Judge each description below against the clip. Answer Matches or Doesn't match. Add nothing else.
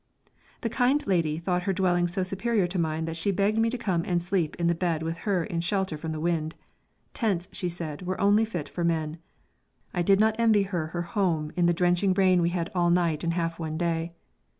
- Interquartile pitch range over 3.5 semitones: Doesn't match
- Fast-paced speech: Matches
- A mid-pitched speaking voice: Matches